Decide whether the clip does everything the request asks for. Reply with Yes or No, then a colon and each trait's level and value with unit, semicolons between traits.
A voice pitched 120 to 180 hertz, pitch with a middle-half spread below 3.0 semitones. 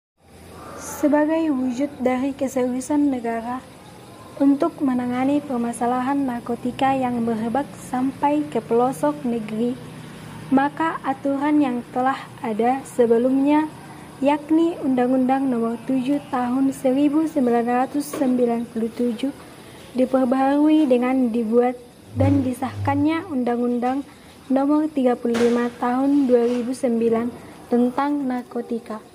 No: very high, 260 Hz; narrow, 2.5 semitones